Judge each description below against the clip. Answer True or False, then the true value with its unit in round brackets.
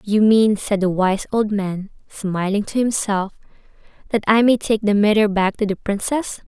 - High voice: True (205 Hz)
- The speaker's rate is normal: True (185 wpm)